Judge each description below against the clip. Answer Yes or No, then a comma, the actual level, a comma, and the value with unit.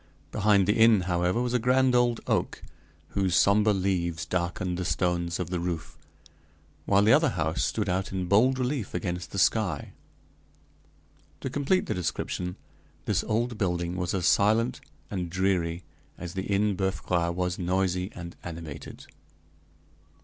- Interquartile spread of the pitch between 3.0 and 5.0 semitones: Yes, average, 3.4 semitones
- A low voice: Yes, very low, 95 Hz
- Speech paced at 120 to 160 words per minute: Yes, average, 150 wpm